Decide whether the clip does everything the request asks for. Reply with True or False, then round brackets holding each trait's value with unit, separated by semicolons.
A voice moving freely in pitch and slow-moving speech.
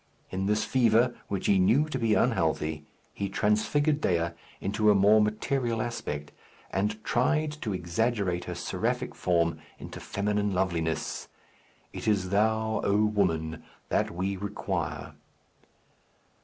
False (3.4 semitones; 130 wpm)